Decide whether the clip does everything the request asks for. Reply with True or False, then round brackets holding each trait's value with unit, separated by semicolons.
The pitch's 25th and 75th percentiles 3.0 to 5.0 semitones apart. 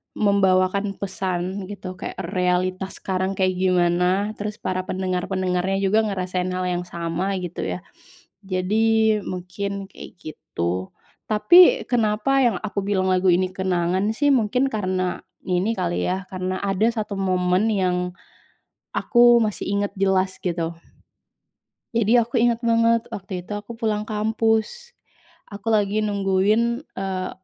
False (2.6 semitones)